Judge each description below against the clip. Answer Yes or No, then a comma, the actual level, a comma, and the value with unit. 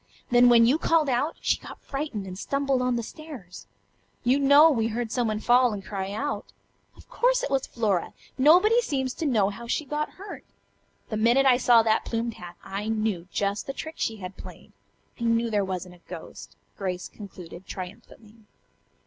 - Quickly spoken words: No, average, 185 wpm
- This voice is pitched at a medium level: No, high, 235 Hz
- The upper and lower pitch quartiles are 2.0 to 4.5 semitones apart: No, average, 5.1 semitones